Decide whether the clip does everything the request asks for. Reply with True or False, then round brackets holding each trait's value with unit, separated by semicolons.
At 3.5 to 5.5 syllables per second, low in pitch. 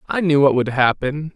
False (5.1 syllables/s; 145 Hz)